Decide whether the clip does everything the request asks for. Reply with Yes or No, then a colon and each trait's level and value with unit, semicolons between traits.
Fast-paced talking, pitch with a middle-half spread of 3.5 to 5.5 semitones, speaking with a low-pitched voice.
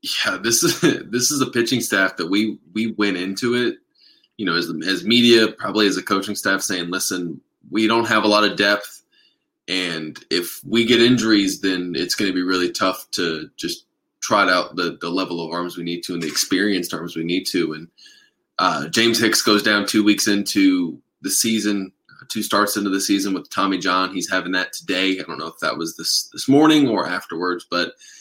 Yes: fast, 210 wpm; average, 4.0 semitones; low, 100 Hz